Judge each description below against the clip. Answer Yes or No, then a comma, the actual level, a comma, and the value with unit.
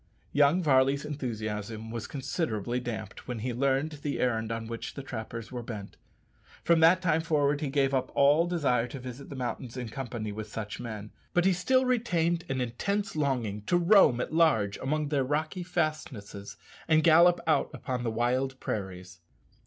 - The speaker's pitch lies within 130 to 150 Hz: Yes, low, 135 Hz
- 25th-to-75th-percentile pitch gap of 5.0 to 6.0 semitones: Yes, wide, 5.5 semitones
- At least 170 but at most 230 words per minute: Yes, average, 175 wpm